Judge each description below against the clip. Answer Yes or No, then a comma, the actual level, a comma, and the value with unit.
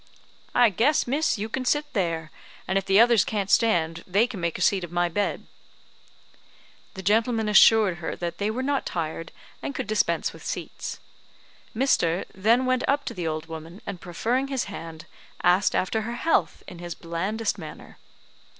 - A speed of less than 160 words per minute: No, average, 180 wpm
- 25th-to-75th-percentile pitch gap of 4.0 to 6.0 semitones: Yes, wide, 5.4 semitones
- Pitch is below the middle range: No, high, 200 Hz